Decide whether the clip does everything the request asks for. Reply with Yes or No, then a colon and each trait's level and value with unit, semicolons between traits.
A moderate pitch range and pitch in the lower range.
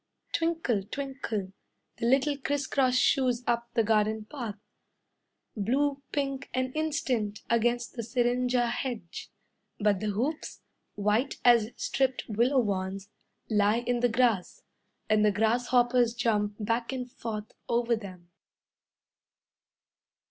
No: average, 3.3 semitones; high, 240 Hz